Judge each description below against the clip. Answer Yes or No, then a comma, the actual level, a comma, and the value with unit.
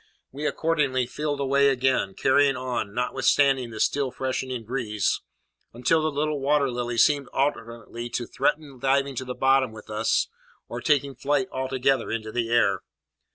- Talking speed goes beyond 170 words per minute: No, average, 155 wpm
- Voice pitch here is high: No, low, 130 Hz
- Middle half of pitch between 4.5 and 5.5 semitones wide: No, average, 2.7 semitones